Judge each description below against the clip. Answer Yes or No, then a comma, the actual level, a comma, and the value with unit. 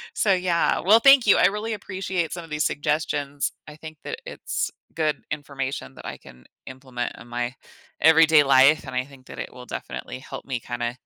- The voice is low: No, medium, 150 Hz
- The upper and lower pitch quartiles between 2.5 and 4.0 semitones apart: No, average, 4.6 semitones